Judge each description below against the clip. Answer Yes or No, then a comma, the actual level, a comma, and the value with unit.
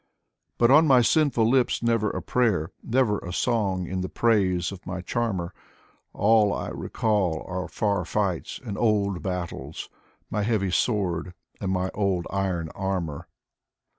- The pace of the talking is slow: No, average, 145 wpm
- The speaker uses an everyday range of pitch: Yes, average, 3.6 semitones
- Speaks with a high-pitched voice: No, low, 100 Hz